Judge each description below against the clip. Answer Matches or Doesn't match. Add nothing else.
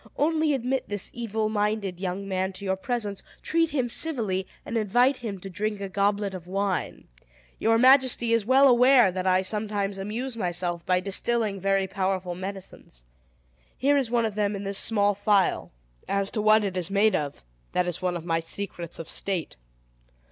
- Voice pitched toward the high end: Matches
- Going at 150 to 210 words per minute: Matches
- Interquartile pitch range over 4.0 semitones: Doesn't match